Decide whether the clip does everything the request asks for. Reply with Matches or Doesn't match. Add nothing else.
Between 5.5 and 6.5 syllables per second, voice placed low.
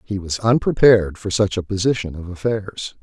Doesn't match